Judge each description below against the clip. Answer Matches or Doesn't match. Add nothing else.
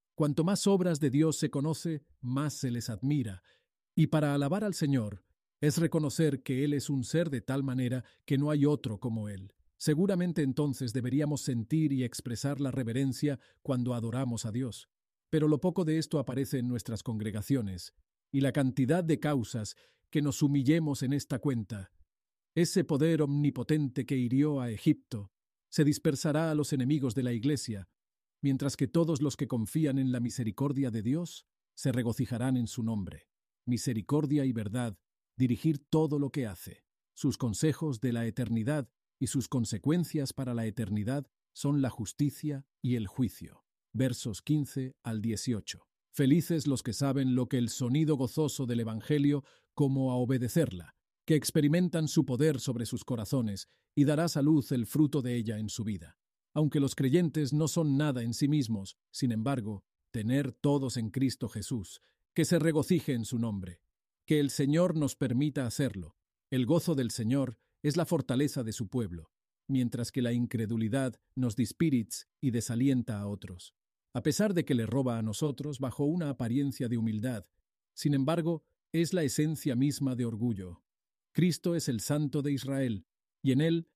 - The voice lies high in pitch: Doesn't match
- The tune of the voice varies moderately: Matches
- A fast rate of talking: Doesn't match